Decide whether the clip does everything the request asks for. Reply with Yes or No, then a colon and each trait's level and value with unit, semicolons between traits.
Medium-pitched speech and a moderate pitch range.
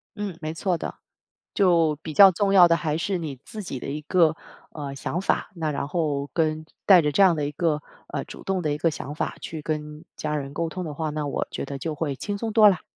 Yes: medium, 160 Hz; average, 3.2 semitones